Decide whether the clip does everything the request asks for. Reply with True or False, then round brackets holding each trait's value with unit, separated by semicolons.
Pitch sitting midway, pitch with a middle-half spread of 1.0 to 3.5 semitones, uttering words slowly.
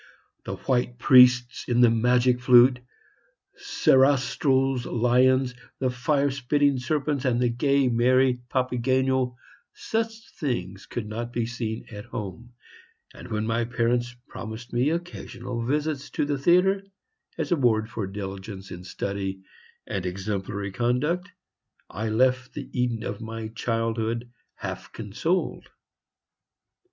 False (125 Hz; 2.8 semitones; 125 wpm)